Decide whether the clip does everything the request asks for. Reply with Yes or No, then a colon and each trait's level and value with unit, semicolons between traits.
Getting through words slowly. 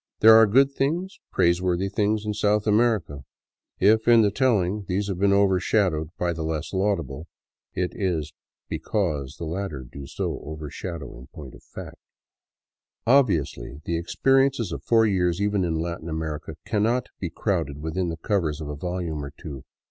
No: average, 165 wpm